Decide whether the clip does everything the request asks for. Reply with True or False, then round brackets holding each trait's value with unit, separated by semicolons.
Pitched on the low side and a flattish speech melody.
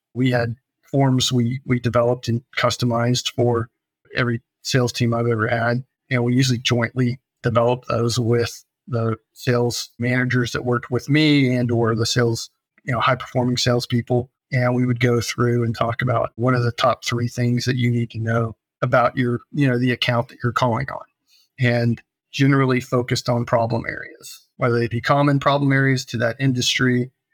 True (120 Hz; 1.2 semitones)